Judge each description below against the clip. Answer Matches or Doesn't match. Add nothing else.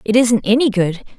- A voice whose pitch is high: Matches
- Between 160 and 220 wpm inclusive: Matches